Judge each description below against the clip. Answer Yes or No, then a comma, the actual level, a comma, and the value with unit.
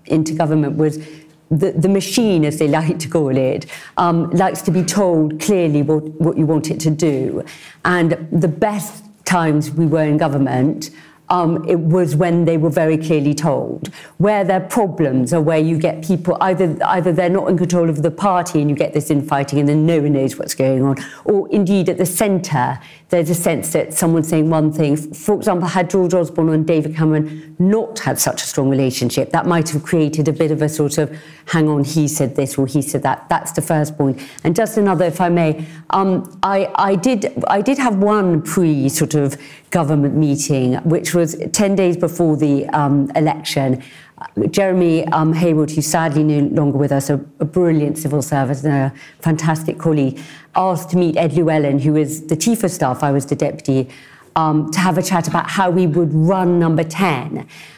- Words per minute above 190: Yes, average, 200 wpm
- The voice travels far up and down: No, average, 2.9 semitones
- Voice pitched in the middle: Yes, medium, 160 Hz